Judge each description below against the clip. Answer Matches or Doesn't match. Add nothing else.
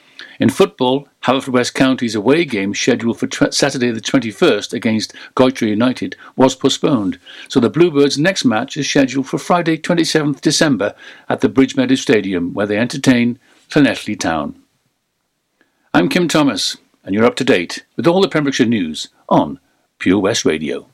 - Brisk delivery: Doesn't match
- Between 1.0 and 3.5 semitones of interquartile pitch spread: Doesn't match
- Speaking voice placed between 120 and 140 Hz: Matches